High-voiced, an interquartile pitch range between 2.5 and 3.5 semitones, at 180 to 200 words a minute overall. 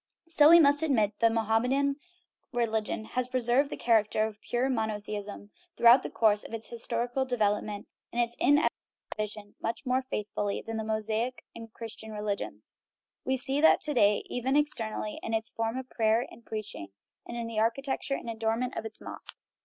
Yes: high, 230 Hz; average, 2.8 semitones; average, 185 wpm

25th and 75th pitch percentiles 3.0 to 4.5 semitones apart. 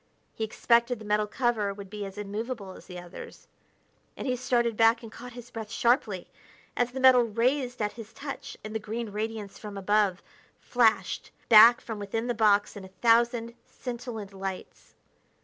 No: narrow, 2.5 semitones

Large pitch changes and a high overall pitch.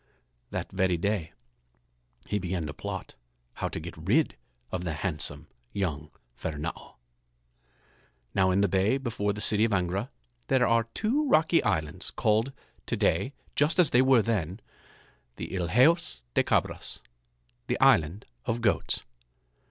No: wide, 6.2 semitones; low, 100 Hz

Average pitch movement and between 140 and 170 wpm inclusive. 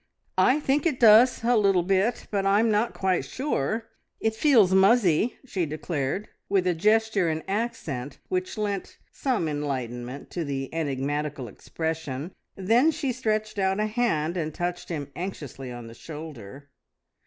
No: wide, 6.9 semitones; average, 150 wpm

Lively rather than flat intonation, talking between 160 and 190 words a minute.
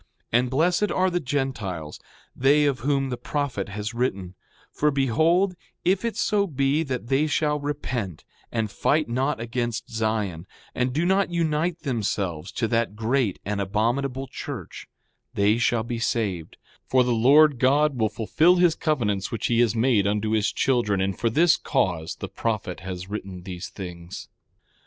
Yes: wide, 5.8 semitones; average, 165 wpm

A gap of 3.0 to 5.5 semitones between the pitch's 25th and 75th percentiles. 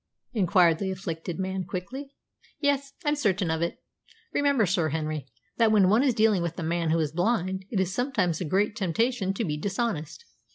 Yes: average, 5.2 semitones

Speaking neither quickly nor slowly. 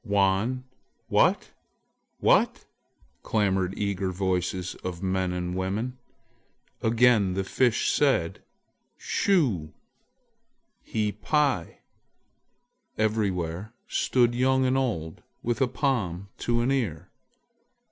No: slow, 95 wpm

